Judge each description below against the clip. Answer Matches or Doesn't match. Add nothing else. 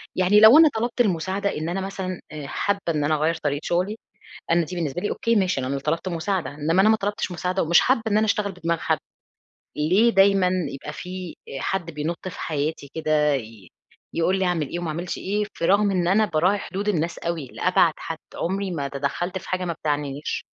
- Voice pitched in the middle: Matches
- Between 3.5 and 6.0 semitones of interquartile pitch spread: Matches